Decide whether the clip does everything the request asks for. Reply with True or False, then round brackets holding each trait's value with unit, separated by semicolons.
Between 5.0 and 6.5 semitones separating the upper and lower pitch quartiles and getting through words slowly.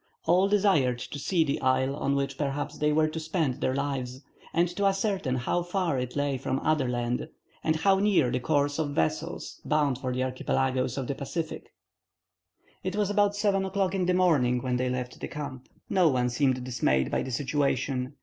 False (5.3 semitones; 195 wpm)